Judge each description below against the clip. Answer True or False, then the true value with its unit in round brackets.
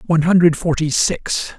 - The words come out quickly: False (150 wpm)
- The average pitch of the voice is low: False (165 Hz)